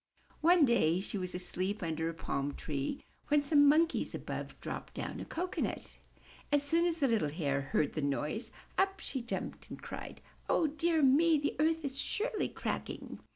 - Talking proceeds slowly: No, average, 175 wpm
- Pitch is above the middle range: Yes, very high, 275 Hz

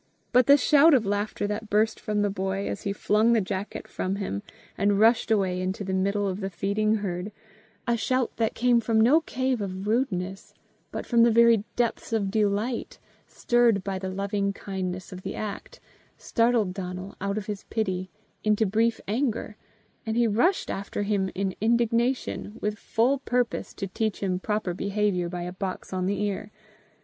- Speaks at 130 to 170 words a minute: No, average, 180 wpm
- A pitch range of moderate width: Yes, average, 3.0 semitones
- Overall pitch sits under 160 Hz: No, high, 210 Hz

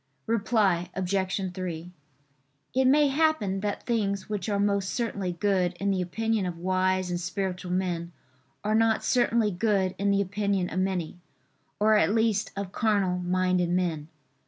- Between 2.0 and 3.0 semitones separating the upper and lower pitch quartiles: Yes, average, 2.7 semitones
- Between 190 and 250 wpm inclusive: No, average, 155 wpm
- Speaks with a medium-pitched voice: No, high, 195 Hz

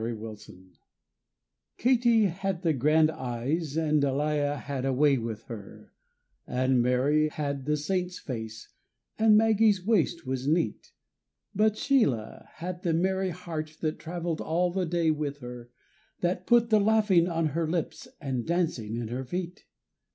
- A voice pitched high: No, medium, 155 Hz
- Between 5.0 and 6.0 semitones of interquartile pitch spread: Yes, wide, 5.4 semitones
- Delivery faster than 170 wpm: No, average, 150 wpm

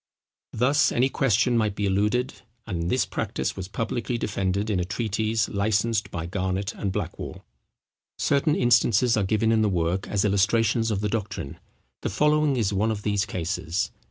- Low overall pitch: Yes, low, 105 Hz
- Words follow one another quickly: No, average, 165 wpm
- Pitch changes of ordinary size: Yes, average, 3.0 semitones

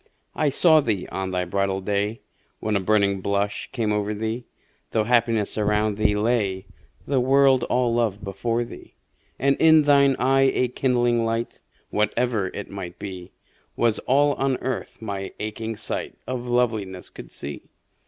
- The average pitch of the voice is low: Yes, low, 110 Hz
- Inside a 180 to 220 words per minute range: No, average, 155 wpm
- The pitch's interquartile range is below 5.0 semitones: Yes, average, 3.7 semitones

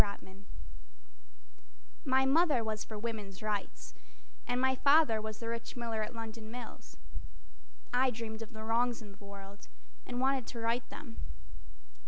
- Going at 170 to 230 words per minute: No, average, 155 wpm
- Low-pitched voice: No, high, 230 Hz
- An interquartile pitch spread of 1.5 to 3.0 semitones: Yes, narrow, 2.4 semitones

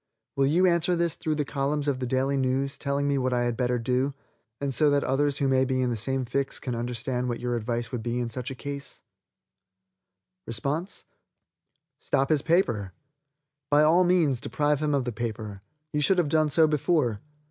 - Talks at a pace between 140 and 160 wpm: No, average, 195 wpm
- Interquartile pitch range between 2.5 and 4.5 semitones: Yes, average, 3.2 semitones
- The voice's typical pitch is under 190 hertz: Yes, low, 135 Hz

